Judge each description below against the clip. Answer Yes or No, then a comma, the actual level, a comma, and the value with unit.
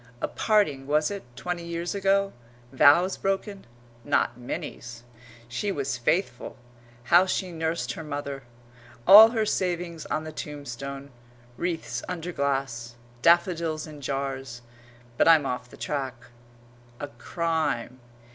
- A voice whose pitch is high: No, medium, 155 Hz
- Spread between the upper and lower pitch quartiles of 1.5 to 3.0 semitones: No, average, 4.7 semitones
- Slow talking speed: Yes, slow, 125 wpm